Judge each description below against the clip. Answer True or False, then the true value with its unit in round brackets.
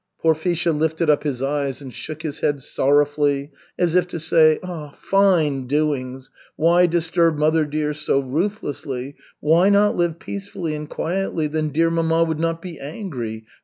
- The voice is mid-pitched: True (155 Hz)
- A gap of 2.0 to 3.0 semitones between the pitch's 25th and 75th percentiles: True (2.6 semitones)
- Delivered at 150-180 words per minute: True (155 wpm)